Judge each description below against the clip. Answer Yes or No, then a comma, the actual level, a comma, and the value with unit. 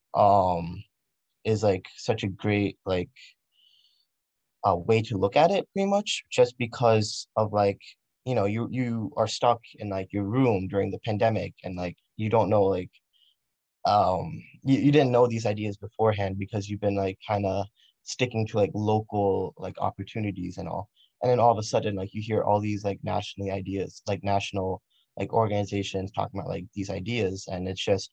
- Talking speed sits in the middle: Yes, average, 185 wpm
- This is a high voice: No, low, 105 Hz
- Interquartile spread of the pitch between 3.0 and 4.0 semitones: No, narrow, 2.4 semitones